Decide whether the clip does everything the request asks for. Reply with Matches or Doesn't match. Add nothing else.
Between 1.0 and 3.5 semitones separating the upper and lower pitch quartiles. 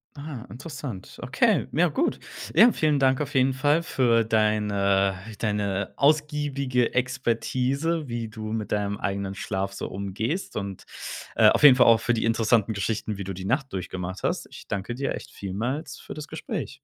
Doesn't match